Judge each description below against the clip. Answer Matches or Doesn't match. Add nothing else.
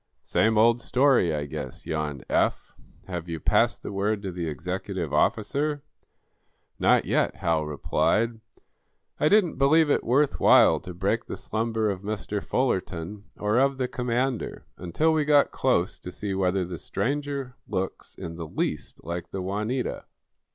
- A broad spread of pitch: Matches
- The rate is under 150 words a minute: Doesn't match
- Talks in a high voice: Doesn't match